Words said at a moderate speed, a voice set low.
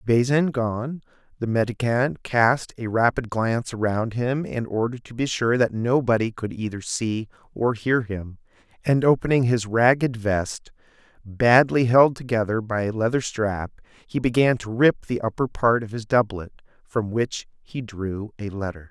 Yes: average, 160 wpm; low, 115 Hz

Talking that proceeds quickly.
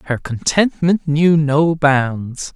No: slow, 115 wpm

